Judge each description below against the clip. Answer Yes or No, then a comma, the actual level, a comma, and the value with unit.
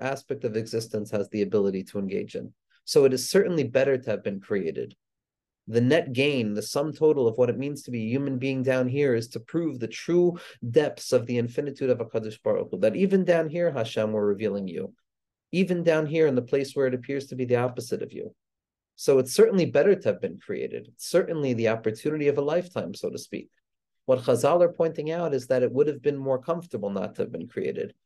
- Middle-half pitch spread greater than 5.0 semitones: Yes, wide, 5.5 semitones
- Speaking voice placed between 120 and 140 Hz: Yes, low, 135 Hz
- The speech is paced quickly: Yes, fast, 225 wpm